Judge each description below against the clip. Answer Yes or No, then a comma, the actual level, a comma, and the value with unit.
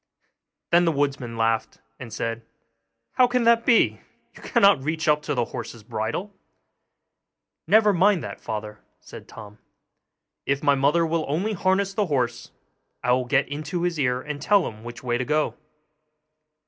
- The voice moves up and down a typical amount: No, wide, 6.9 semitones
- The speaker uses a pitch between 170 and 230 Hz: No, medium, 145 Hz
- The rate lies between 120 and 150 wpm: No, average, 160 wpm